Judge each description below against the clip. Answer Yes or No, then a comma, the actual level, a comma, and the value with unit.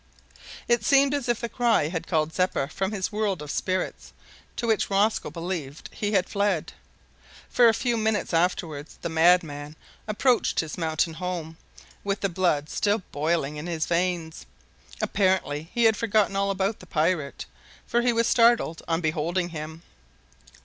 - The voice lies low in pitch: No, medium, 185 Hz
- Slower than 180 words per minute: Yes, average, 160 wpm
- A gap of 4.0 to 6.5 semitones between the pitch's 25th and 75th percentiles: Yes, average, 4.9 semitones